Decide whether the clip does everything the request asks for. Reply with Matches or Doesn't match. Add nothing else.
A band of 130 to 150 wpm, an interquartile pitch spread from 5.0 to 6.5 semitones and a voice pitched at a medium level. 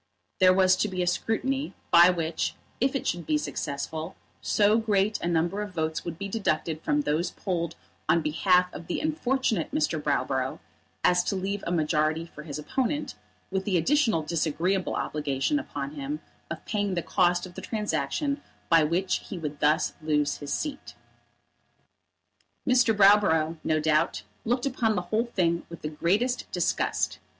Doesn't match